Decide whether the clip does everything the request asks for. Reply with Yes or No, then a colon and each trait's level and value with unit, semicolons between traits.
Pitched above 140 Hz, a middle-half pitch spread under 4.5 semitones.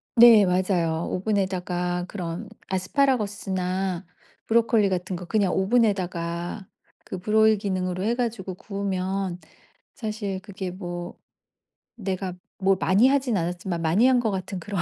Yes: high, 190 Hz; average, 2.9 semitones